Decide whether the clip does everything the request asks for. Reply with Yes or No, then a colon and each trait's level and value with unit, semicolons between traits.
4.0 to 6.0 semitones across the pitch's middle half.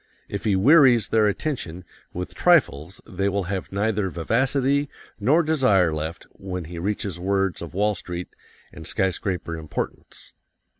Yes: average, 4.6 semitones